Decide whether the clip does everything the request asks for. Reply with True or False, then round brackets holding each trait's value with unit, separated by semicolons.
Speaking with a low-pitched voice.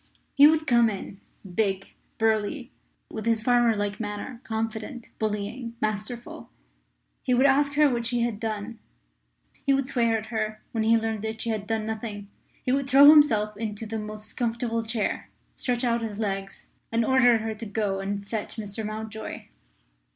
False (225 Hz)